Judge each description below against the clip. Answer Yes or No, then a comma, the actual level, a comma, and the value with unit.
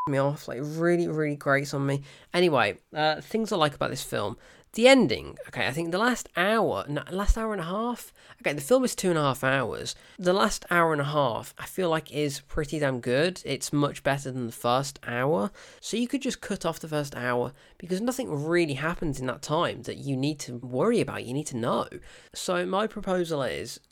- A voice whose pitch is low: No, medium, 155 Hz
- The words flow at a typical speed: No, fast, 220 wpm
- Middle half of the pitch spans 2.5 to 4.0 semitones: No, average, 5.0 semitones